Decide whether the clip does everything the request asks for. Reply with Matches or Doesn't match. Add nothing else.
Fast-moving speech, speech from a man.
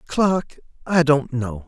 Doesn't match